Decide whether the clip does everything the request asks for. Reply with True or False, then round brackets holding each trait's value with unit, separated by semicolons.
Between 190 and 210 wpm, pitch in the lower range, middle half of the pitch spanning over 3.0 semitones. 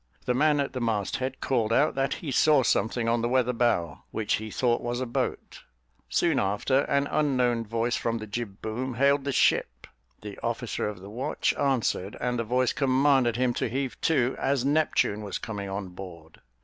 True (195 wpm; 120 Hz; 3.6 semitones)